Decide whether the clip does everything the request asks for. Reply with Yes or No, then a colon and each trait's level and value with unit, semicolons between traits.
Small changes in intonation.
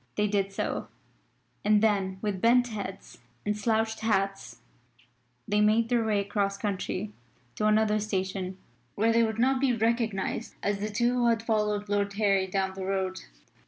Yes: narrow, 2.1 semitones